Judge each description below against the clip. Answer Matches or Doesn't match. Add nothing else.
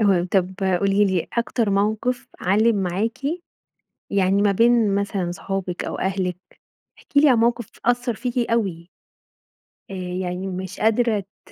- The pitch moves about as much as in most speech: Matches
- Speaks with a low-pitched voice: Doesn't match